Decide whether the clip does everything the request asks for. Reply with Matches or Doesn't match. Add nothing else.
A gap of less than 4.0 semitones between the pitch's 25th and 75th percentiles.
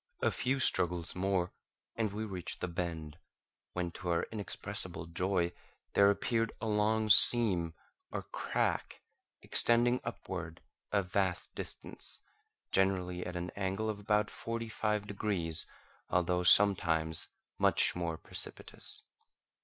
Matches